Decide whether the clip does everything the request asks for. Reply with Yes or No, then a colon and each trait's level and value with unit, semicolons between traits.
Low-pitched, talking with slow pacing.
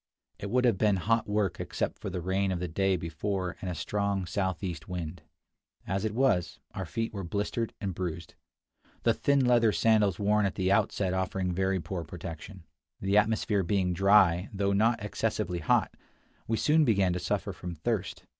No: very low, 95 Hz; average, 180 wpm